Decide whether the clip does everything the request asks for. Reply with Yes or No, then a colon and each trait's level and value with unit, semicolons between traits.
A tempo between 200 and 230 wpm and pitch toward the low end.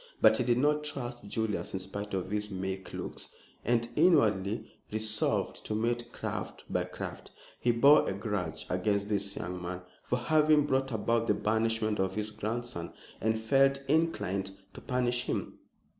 No: average, 160 wpm; low, 110 Hz